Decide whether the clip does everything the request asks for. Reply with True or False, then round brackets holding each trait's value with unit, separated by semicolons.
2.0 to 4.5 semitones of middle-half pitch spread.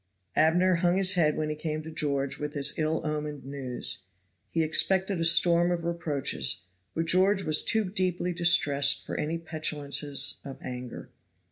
True (3.0 semitones)